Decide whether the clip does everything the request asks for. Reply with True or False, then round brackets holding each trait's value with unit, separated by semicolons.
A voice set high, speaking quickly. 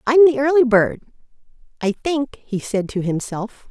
False (245 Hz; 160 wpm)